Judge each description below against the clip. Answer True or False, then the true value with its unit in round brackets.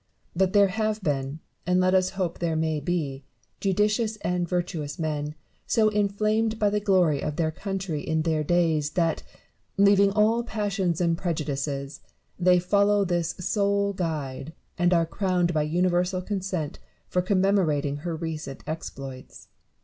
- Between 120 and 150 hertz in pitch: False (175 Hz)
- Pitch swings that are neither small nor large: True (4.1 semitones)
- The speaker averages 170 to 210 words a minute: False (145 wpm)